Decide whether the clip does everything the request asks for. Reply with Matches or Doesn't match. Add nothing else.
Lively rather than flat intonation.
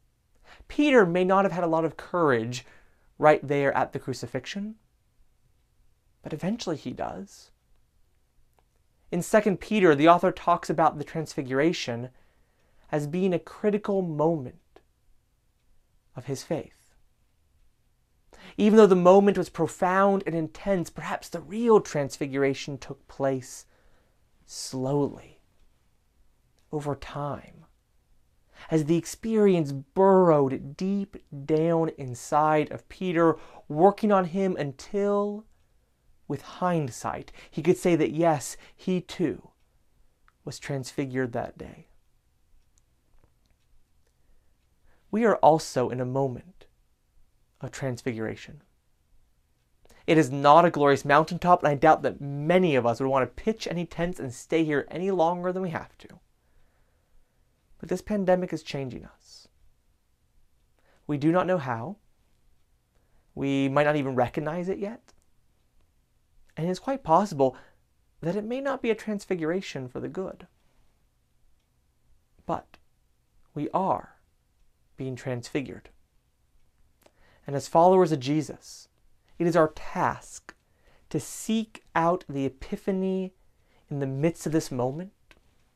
Matches